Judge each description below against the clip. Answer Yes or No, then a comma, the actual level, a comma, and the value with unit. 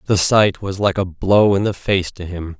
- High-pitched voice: No, very low, 95 Hz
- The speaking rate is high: Yes, fast, 255 wpm